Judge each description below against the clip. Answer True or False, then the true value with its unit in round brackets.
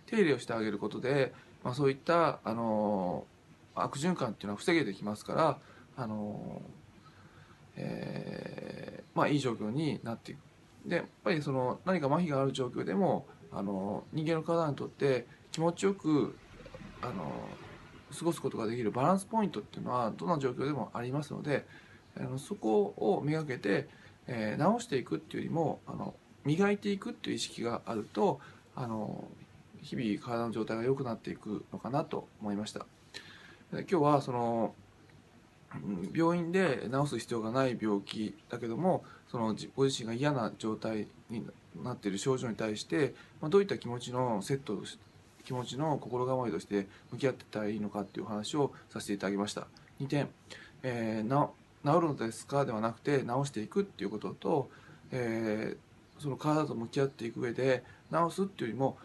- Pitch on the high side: False (125 Hz)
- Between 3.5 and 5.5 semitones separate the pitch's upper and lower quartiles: True (5.2 semitones)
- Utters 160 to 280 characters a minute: False (345 characters per minute)